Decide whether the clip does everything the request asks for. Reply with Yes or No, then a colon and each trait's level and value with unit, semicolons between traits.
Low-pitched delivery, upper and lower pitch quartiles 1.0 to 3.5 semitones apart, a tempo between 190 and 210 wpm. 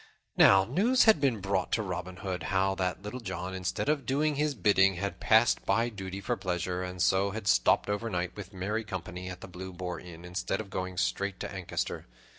Yes: very low, 95 Hz; average, 3.1 semitones; fast, 205 wpm